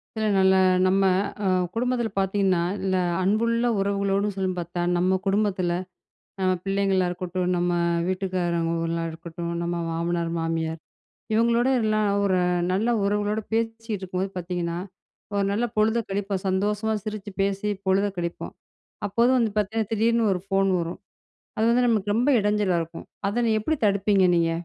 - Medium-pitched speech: No, high, 195 Hz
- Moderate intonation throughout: Yes, average, 3.0 semitones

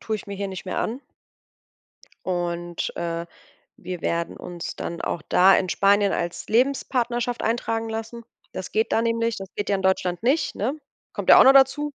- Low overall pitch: No, high, 205 Hz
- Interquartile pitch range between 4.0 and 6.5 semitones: Yes, average, 4.7 semitones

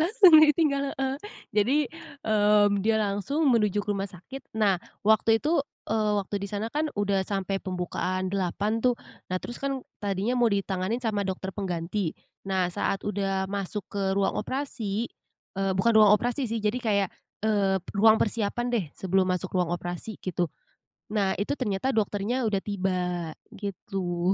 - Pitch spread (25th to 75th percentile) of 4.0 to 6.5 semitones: No, average, 2.8 semitones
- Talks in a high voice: Yes, high, 205 Hz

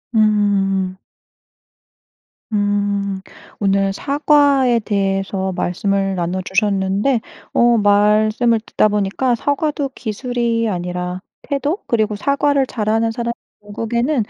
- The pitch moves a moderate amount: Yes, average, 3.5 semitones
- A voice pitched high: Yes, high, 210 Hz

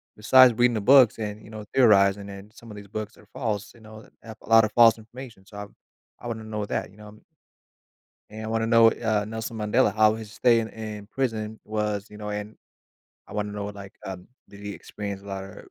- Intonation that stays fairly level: Yes, narrow, 1.6 semitones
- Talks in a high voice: No, low, 110 Hz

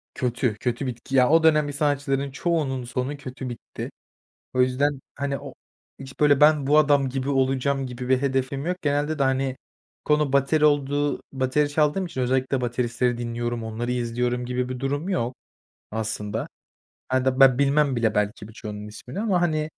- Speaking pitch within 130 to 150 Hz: Yes, low, 135 Hz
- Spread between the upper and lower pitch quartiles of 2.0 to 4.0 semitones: Yes, average, 2.7 semitones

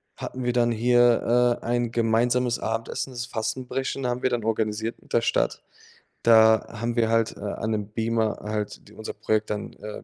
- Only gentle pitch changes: Yes, narrow, 1.6 semitones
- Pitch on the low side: Yes, low, 115 Hz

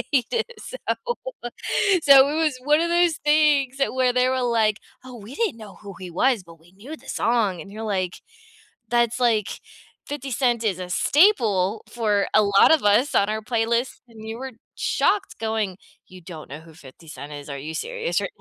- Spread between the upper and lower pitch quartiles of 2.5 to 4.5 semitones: No, wide, 5.5 semitones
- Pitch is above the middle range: Yes, high, 225 Hz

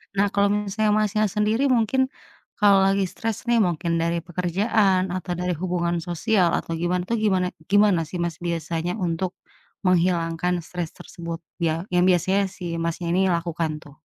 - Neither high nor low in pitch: Yes, medium, 180 Hz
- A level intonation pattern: No, average, 3.0 semitones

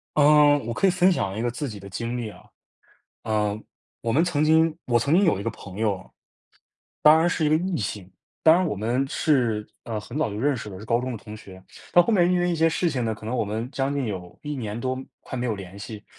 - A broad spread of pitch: Yes, wide, 6.3 semitones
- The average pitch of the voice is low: Yes, low, 120 Hz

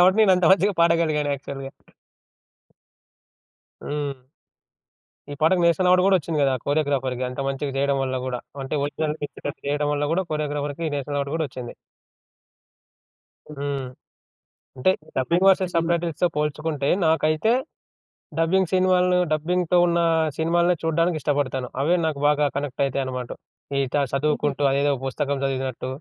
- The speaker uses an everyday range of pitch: Yes, average, 3.4 semitones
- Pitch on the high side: No, medium, 150 Hz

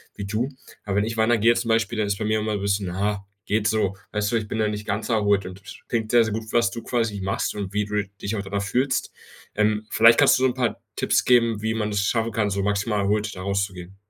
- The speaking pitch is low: Yes, low, 105 Hz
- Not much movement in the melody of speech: Yes, narrow, 2.1 semitones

